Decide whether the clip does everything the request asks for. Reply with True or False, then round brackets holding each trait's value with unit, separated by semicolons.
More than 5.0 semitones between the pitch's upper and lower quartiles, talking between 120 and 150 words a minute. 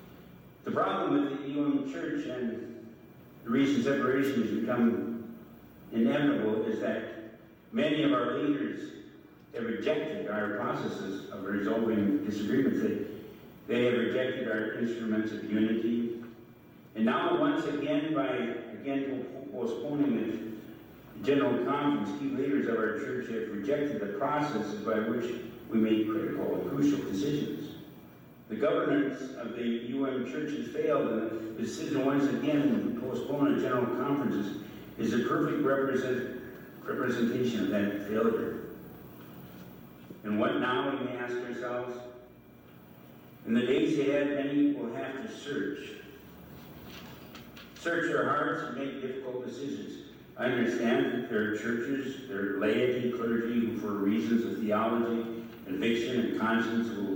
False (3.6 semitones; 135 wpm)